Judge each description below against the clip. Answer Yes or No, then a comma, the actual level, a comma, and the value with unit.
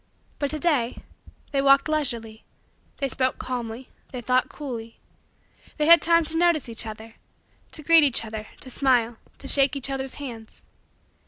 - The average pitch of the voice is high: Yes, very high, 265 Hz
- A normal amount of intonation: Yes, average, 4.1 semitones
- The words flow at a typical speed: Yes, average, 160 wpm